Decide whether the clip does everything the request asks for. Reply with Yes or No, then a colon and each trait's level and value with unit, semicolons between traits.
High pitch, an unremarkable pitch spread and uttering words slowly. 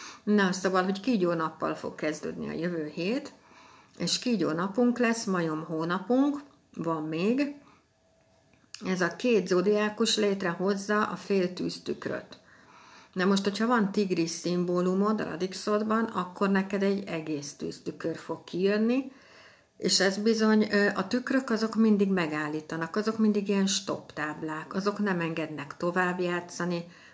No: high, 195 Hz; average, 3.8 semitones; average, 130 wpm